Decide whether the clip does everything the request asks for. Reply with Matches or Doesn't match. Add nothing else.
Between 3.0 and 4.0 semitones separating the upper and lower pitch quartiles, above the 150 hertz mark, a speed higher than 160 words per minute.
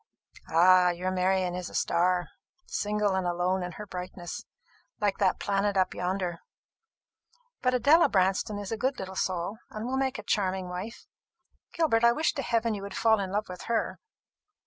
Matches